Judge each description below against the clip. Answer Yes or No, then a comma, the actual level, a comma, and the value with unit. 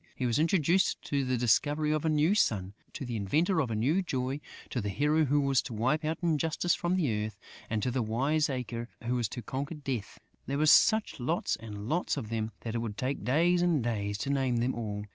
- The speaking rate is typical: No, fast, 225 wpm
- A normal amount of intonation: Yes, average, 5.0 semitones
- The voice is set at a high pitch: No, low, 130 Hz